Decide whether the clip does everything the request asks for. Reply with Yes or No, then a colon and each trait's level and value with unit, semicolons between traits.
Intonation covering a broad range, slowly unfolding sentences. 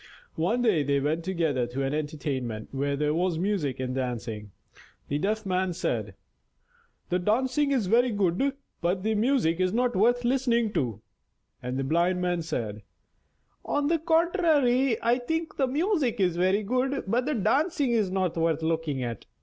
No: wide, 8.7 semitones; average, 165 wpm